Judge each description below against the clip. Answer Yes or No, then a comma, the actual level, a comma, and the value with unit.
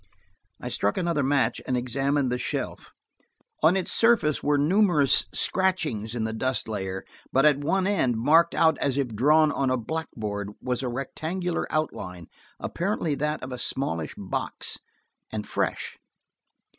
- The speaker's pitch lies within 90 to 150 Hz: Yes, medium, 140 Hz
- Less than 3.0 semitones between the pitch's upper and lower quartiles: No, average, 5.0 semitones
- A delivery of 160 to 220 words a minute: No, average, 150 wpm